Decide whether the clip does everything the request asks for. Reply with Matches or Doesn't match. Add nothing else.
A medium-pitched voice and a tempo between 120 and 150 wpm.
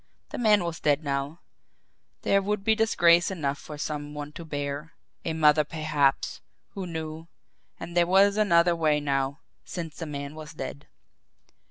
Doesn't match